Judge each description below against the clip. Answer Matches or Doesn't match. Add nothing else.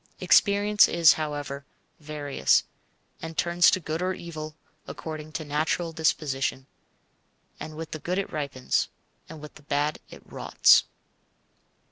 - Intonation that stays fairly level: Matches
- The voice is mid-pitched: Matches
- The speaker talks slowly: Matches